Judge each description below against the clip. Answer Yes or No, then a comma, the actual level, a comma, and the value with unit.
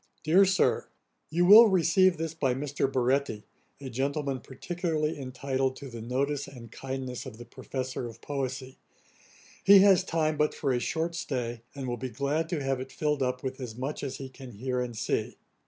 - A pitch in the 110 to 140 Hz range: Yes, low, 135 Hz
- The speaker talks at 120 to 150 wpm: No, average, 190 wpm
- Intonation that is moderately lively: Yes, average, 3.4 semitones